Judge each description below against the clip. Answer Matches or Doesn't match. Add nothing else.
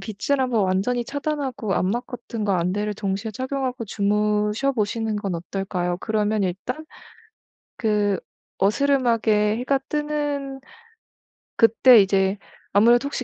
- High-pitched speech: Matches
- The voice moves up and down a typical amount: Matches